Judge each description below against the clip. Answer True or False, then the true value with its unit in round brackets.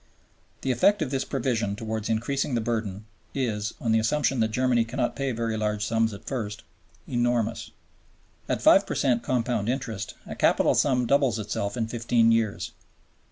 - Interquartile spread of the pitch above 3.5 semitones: False (2.5 semitones)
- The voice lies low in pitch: True (115 Hz)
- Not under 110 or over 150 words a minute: False (165 wpm)